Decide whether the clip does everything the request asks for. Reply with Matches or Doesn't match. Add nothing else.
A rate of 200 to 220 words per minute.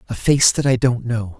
Doesn't match